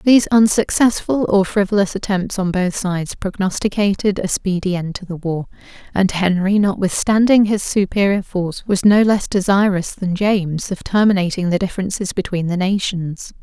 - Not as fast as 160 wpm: Yes, average, 150 wpm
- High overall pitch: Yes, high, 195 Hz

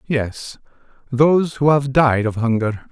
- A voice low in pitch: Yes, low, 130 Hz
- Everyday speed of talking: Yes, average, 145 wpm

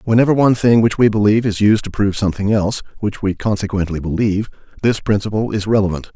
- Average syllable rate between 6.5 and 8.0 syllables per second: Yes, 6.9 syllables/s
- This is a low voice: Yes, low, 105 Hz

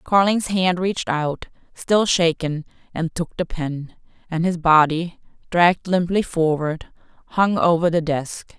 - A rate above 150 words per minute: No, average, 140 wpm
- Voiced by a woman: Yes, female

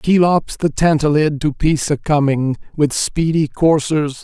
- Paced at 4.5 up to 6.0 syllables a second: No, 4.0 syllables/s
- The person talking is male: Yes, male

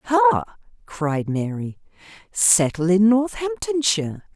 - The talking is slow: Yes, slow, 85 wpm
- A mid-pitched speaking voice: No, high, 200 Hz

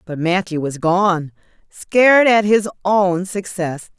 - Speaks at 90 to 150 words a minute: Yes, slow, 135 wpm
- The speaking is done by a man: No, female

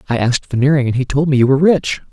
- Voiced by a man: Yes, male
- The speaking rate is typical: No, fast, 285 wpm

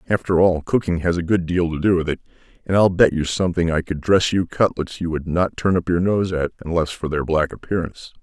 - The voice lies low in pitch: Yes, very low, 85 Hz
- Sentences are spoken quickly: Yes, fast, 250 wpm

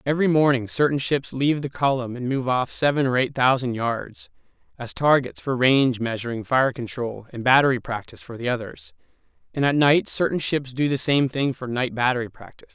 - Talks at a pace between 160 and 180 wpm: No, average, 195 wpm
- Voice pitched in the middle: No, low, 130 Hz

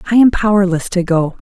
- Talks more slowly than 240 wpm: Yes, fast, 205 wpm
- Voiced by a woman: Yes, female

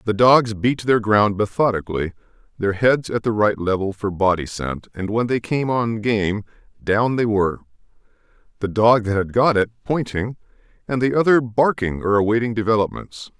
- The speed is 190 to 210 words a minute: No, average, 170 wpm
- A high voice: No, low, 110 Hz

